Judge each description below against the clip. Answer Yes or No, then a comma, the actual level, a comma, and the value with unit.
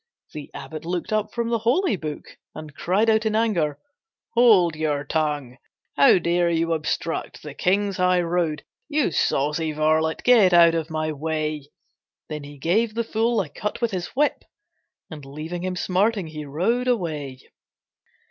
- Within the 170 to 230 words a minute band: No, average, 155 wpm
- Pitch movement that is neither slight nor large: No, wide, 5.7 semitones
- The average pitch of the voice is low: No, medium, 170 Hz